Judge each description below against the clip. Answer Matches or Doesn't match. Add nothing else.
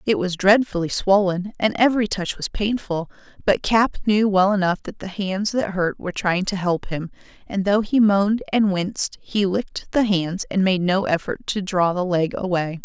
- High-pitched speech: Matches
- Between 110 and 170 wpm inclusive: Doesn't match